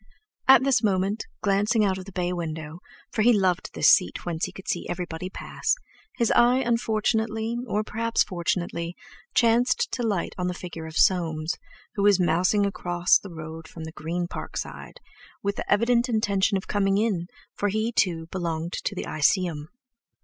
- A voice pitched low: No, high, 190 Hz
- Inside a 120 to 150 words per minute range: No, average, 170 wpm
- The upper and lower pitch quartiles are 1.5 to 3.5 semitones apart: No, average, 4.1 semitones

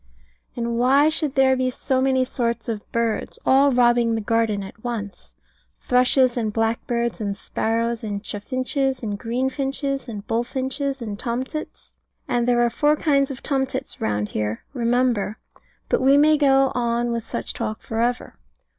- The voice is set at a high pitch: Yes, high, 240 Hz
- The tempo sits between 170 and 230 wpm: No, average, 155 wpm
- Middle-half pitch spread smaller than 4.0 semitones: Yes, average, 2.8 semitones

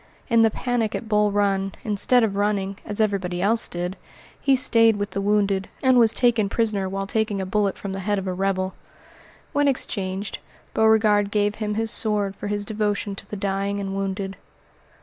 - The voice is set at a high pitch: Yes, high, 205 Hz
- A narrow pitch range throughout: Yes, narrow, 2.0 semitones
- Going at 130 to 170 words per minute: No, average, 190 wpm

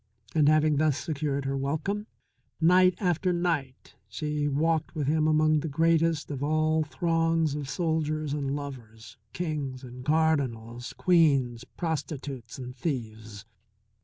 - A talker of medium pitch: Yes, medium, 150 Hz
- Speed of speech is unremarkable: No, slow, 130 wpm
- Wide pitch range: No, average, 3.0 semitones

